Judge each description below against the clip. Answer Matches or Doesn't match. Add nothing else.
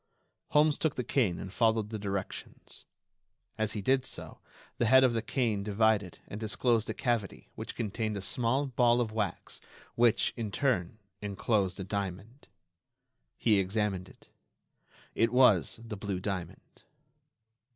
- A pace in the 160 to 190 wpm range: Doesn't match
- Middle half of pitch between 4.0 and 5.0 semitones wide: Doesn't match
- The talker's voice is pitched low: Matches